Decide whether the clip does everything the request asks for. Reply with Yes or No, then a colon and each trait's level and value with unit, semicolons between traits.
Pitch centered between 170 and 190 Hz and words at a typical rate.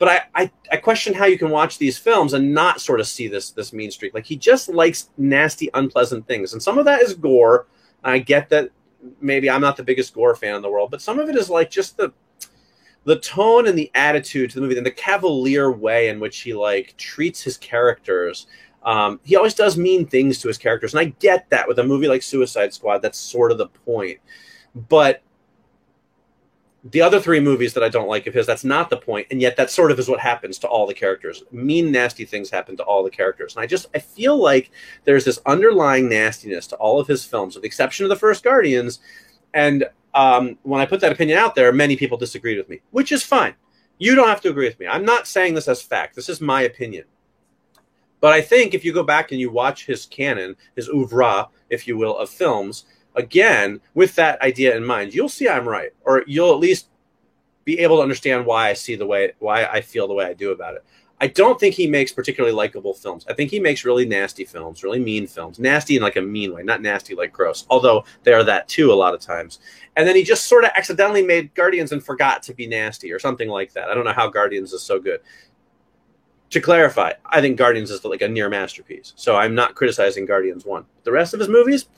No: medium, 185 Hz; fast, 235 wpm